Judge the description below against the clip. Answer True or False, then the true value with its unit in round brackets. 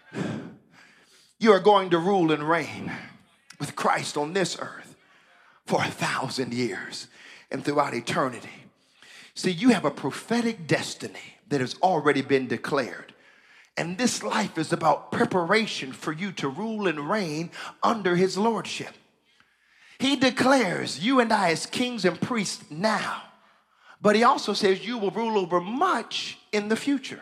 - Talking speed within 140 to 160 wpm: True (150 wpm)